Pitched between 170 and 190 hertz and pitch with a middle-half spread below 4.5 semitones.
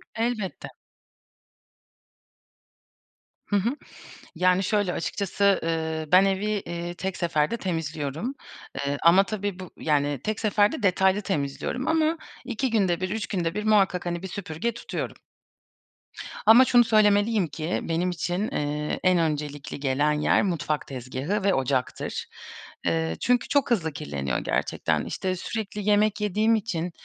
No: medium, 185 Hz; average, 4.9 semitones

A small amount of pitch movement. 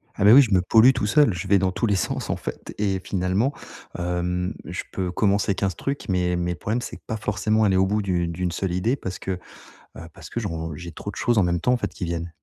No: average, 3.3 semitones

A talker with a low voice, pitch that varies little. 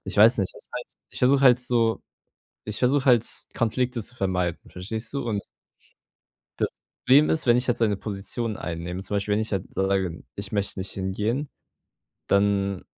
No: low, 105 Hz; average, 3.9 semitones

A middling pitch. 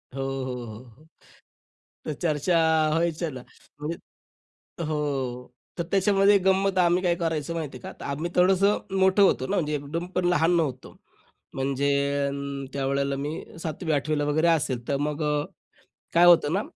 Yes: medium, 155 Hz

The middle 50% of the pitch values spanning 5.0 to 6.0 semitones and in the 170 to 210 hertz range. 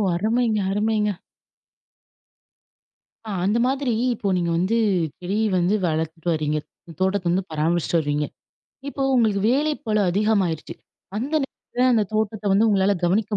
No: average, 4.2 semitones; high, 200 Hz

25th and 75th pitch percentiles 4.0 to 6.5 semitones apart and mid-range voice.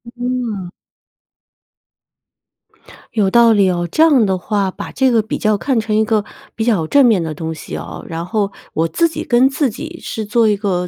No: average, 4.4 semitones; high, 215 Hz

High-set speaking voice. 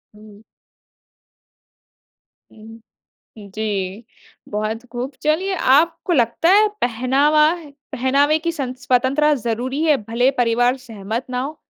Yes: very high, 255 Hz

